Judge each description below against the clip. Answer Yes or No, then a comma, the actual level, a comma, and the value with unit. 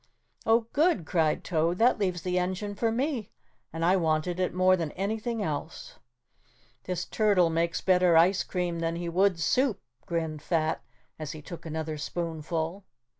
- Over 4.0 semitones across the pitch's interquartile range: No, average, 3.2 semitones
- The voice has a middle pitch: Yes, medium, 175 Hz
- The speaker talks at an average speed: Yes, average, 160 wpm